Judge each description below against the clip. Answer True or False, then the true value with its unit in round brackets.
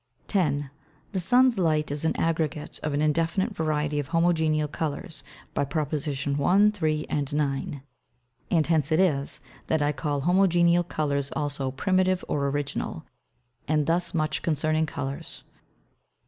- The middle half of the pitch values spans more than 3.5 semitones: False (2.8 semitones)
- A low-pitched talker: False (155 Hz)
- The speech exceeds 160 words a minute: False (140 wpm)